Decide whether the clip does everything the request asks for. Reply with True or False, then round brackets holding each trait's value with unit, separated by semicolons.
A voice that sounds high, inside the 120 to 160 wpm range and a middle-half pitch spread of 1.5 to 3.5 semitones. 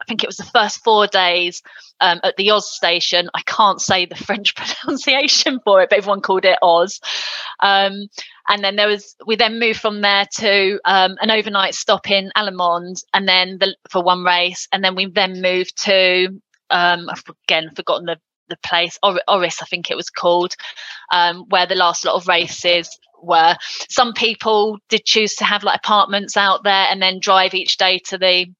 False (195 Hz; 195 wpm; 2.5 semitones)